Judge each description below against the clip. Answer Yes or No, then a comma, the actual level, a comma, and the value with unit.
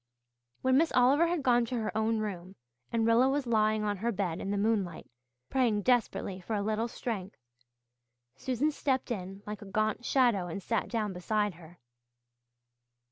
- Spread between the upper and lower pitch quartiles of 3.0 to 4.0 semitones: Yes, average, 3.6 semitones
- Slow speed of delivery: No, average, 170 wpm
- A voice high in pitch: Yes, high, 215 Hz